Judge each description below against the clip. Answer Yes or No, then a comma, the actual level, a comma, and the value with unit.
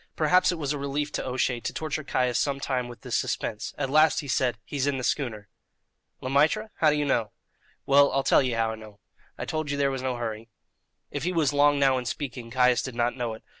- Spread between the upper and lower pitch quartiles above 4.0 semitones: No, average, 3.1 semitones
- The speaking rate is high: Yes, fast, 245 wpm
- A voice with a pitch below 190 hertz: Yes, low, 135 Hz